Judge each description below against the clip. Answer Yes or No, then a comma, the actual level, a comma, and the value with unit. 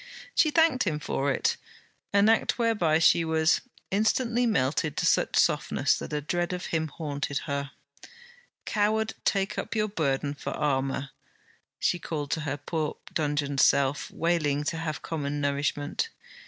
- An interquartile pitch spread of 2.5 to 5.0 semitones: No, wide, 5.4 semitones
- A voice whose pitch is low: No, medium, 155 Hz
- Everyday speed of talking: Yes, average, 150 wpm